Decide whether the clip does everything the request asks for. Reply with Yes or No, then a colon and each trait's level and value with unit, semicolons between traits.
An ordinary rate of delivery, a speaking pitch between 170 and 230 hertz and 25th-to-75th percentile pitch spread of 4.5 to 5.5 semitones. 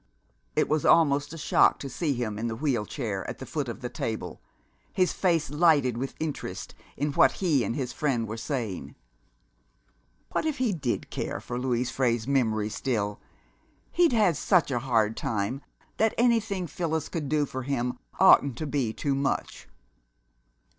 No: average, 170 wpm; low, 135 Hz; average, 5.0 semitones